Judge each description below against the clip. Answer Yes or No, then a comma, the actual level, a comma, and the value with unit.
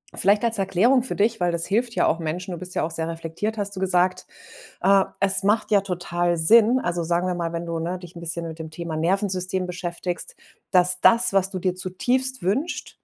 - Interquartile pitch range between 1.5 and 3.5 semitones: Yes, average, 2.9 semitones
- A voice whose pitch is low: No, medium, 185 Hz